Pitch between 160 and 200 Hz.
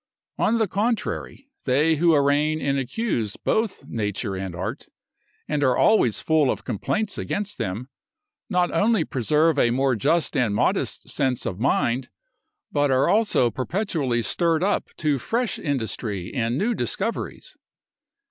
No: medium, 140 Hz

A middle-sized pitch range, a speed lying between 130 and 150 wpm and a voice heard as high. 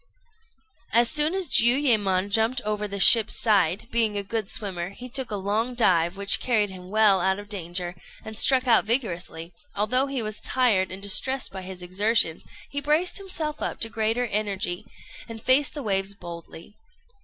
No: average, 4.4 semitones; average, 180 wpm; high, 215 Hz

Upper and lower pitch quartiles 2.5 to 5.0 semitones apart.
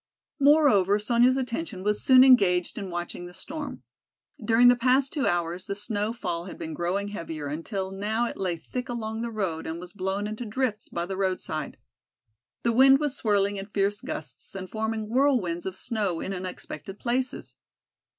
Yes: average, 4.7 semitones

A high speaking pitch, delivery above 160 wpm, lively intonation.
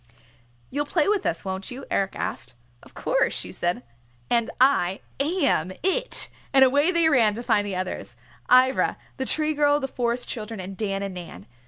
Yes: high, 245 Hz; average, 180 wpm; wide, 6.8 semitones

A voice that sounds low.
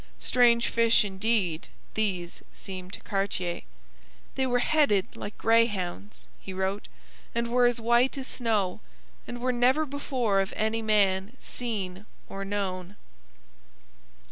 No: high, 215 Hz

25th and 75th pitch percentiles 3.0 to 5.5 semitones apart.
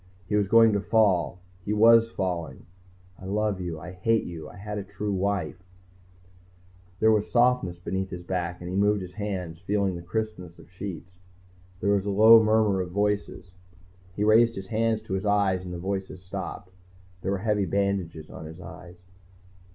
No: narrow, 2.6 semitones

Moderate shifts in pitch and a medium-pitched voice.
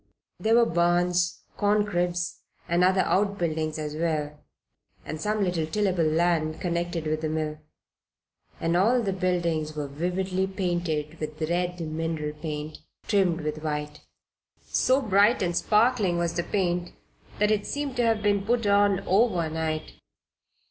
Yes: average, 4.1 semitones; medium, 175 Hz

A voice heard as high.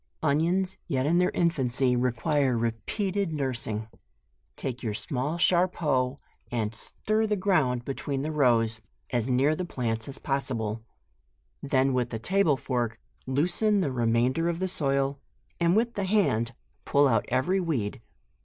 No: low, 135 Hz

